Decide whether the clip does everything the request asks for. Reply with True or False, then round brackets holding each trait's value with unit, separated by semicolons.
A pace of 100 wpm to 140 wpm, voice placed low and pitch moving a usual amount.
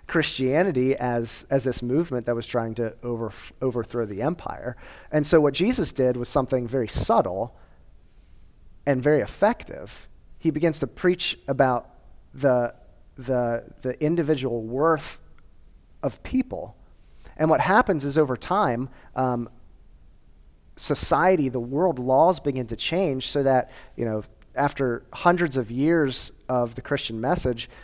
True (135 wpm; 130 Hz; 3.8 semitones)